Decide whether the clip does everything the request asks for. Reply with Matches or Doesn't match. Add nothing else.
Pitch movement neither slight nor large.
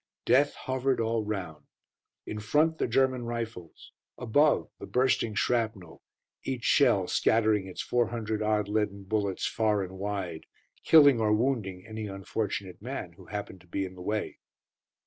Matches